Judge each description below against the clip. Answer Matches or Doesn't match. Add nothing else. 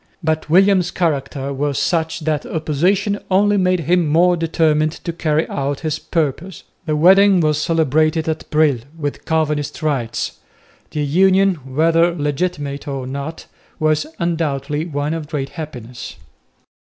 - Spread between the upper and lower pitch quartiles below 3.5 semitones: Matches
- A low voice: Doesn't match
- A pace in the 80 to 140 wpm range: Matches